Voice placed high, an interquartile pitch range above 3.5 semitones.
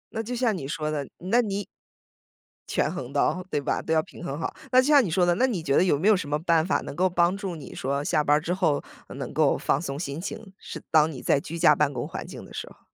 No: medium, 165 Hz; average, 4.6 semitones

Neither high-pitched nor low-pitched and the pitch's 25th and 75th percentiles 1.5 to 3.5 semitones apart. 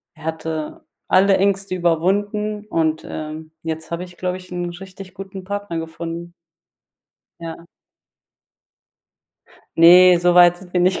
Yes: medium, 175 Hz; narrow, 2.6 semitones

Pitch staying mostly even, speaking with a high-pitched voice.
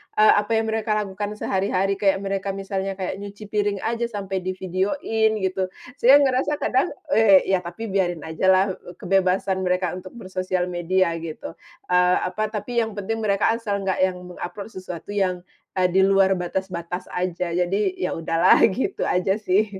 Yes: narrow, 2.3 semitones; high, 195 Hz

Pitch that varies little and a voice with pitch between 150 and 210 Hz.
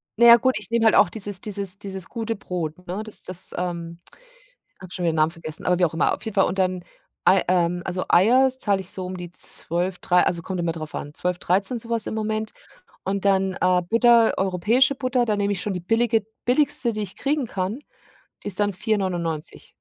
No: average, 3.7 semitones; high, 190 Hz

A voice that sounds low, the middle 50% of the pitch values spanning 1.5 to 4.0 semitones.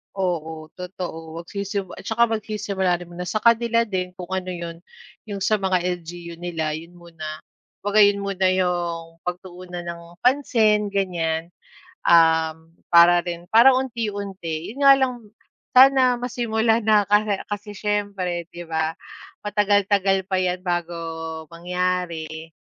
No: medium, 185 Hz; average, 3.4 semitones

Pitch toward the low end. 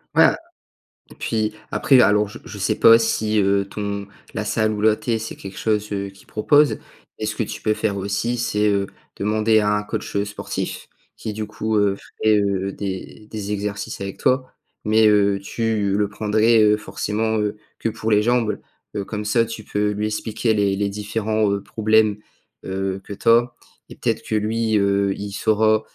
Yes: low, 105 Hz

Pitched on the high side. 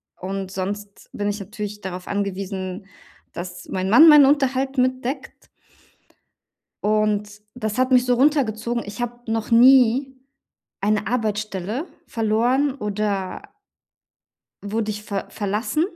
Yes: high, 215 Hz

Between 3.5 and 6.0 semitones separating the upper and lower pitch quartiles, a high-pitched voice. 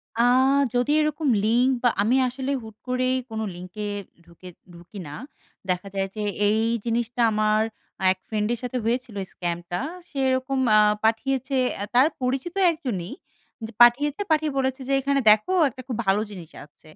Yes: average, 4.1 semitones; high, 235 Hz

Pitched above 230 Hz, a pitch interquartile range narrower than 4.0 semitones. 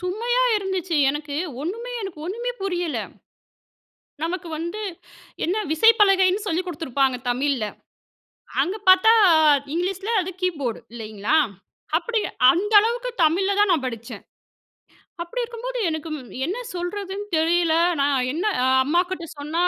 No: very high, 360 Hz; average, 4.7 semitones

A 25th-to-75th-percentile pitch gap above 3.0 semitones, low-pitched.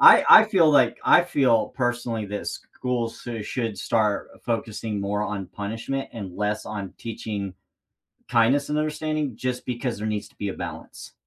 Yes: average, 3.6 semitones; low, 115 Hz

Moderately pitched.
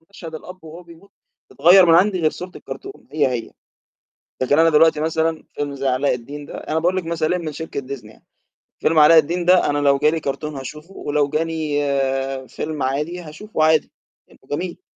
Yes: medium, 155 Hz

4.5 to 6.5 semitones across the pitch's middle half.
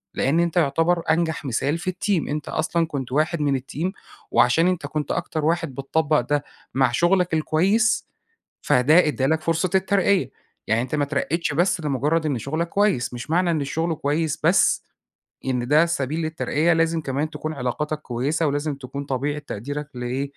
No: average, 3.3 semitones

